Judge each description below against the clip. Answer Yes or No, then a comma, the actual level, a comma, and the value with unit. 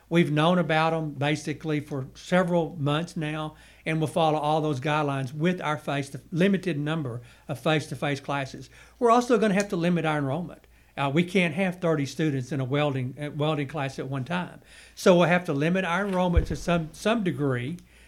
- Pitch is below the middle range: No, medium, 155 Hz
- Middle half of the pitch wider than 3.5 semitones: No, average, 3.1 semitones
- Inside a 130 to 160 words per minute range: No, average, 190 wpm